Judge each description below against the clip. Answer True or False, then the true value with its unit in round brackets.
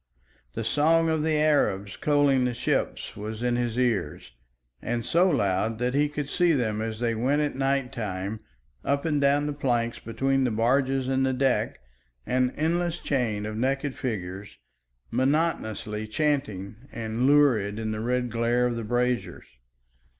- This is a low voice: True (125 Hz)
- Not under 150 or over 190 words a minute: True (160 wpm)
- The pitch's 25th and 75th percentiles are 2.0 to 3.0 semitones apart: False (4.4 semitones)